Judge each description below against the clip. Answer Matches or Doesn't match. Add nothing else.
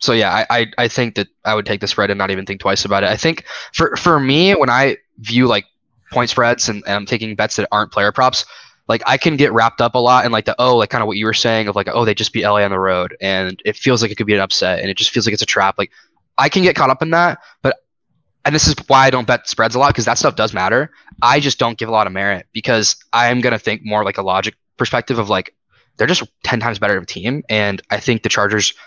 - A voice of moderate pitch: Doesn't match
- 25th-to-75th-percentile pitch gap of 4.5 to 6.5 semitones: Doesn't match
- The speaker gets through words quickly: Matches